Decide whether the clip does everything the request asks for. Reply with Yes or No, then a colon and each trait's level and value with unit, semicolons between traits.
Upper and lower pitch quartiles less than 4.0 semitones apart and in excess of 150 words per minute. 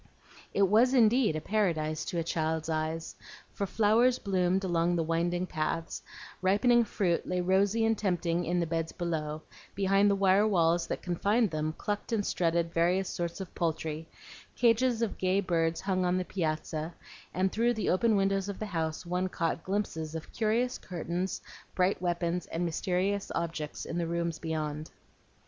Yes: average, 3.4 semitones; average, 165 wpm